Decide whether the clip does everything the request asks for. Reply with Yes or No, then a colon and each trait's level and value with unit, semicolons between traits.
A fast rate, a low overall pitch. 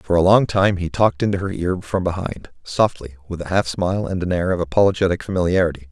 Yes: fast, 225 wpm; very low, 90 Hz